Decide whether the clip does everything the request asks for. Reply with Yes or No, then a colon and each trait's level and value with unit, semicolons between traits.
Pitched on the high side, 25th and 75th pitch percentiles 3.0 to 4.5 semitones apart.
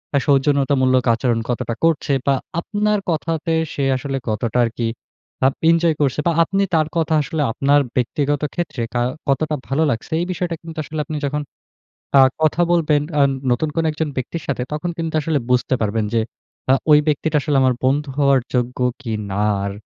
No: medium, 145 Hz; average, 3.7 semitones